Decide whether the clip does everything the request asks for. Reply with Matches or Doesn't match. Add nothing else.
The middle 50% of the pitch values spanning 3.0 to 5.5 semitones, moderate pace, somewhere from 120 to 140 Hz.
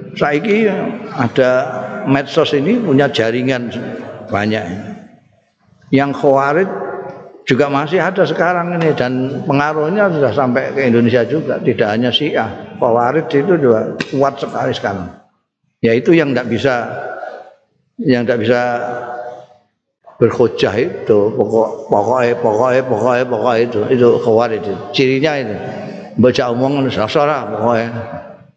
Matches